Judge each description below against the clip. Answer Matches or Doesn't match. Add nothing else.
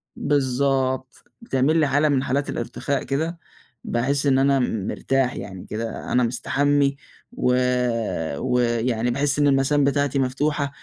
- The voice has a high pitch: Doesn't match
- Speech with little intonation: Matches